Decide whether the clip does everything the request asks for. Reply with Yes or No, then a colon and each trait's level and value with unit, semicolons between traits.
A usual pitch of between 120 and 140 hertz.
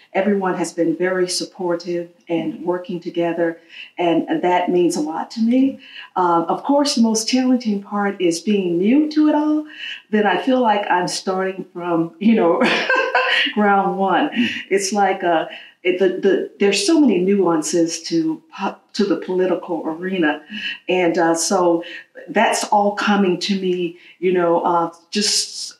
No: high, 190 Hz